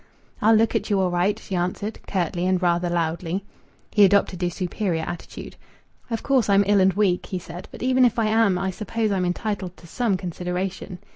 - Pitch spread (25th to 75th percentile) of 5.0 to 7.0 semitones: No, average, 3.0 semitones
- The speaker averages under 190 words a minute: No, average, 200 wpm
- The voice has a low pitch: No, high, 190 Hz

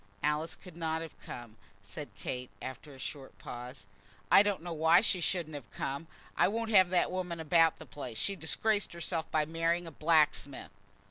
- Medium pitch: Yes, medium, 160 Hz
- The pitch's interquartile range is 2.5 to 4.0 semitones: Yes, average, 3.5 semitones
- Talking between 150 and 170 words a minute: No, average, 185 wpm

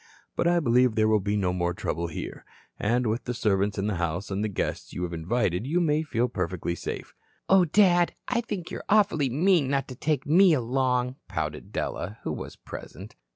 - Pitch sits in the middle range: No, low, 125 Hz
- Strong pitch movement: Yes, wide, 7.8 semitones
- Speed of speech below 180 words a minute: No, average, 200 wpm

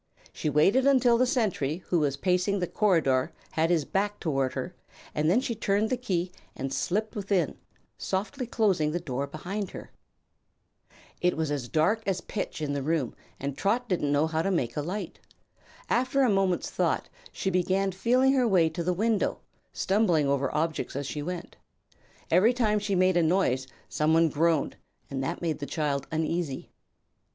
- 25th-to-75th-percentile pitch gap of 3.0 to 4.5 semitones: No, average, 5.3 semitones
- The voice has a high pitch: No, medium, 175 Hz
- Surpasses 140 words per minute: Yes, average, 175 wpm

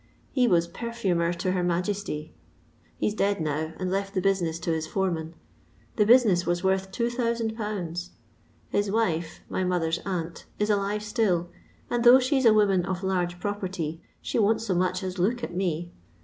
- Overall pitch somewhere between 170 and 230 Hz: Yes, high, 190 Hz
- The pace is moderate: Yes, average, 175 wpm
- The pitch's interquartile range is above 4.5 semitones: No, average, 3.3 semitones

